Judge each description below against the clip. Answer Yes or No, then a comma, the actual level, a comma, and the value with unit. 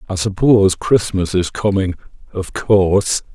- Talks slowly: Yes, slow, 125 wpm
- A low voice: Yes, very low, 95 Hz